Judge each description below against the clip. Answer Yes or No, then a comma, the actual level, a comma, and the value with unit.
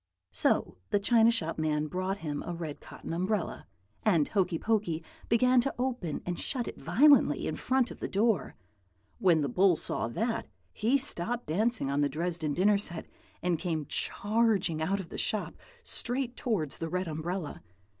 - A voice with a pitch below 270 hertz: Yes, medium, 185 Hz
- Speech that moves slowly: No, average, 170 wpm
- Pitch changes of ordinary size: No, wide, 5.9 semitones